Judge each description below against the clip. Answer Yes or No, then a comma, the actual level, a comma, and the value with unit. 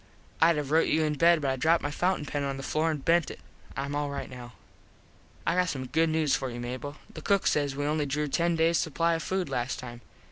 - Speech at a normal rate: No, fast, 245 wpm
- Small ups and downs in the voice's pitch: No, average, 3.1 semitones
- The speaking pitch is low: No, medium, 150 Hz